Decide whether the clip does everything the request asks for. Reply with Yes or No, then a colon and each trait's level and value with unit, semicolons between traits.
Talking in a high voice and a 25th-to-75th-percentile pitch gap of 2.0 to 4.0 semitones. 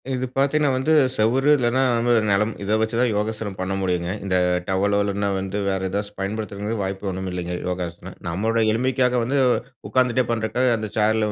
No: low, 105 Hz; average, 3.7 semitones